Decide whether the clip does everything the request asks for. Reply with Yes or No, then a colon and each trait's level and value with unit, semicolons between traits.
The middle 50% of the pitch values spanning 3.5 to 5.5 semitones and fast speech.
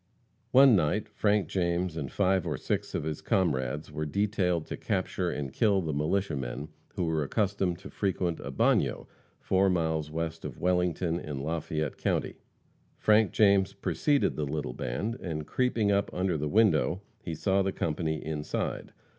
No: average, 4.3 semitones; average, 165 wpm